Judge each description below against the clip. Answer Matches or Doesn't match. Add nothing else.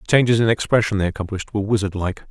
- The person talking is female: Doesn't match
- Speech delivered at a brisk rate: Matches